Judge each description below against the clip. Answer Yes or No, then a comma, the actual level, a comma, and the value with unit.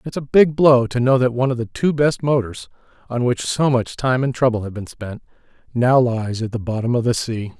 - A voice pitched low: Yes, low, 125 Hz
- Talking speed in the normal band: No, fast, 245 wpm